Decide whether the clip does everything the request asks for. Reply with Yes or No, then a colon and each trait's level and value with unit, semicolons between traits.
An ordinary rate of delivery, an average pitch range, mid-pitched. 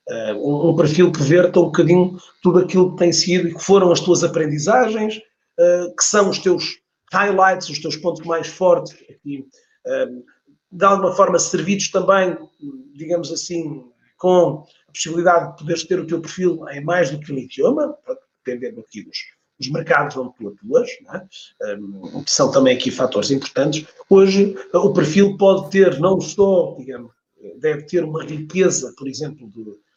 Yes: average, 160 wpm; average, 3.5 semitones; medium, 175 Hz